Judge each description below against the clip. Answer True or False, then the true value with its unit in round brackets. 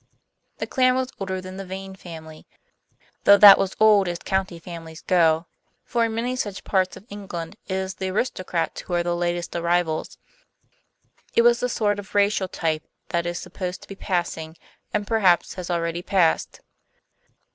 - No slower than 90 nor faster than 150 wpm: False (170 wpm)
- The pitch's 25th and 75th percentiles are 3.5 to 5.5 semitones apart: False (2.9 semitones)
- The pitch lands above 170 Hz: True (185 Hz)